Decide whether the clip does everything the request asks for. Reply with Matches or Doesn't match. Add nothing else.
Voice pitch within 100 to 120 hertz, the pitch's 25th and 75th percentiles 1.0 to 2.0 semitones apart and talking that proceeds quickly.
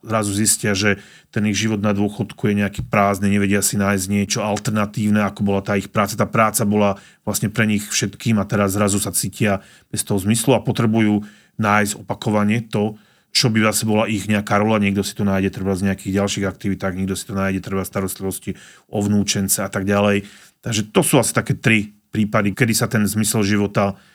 Matches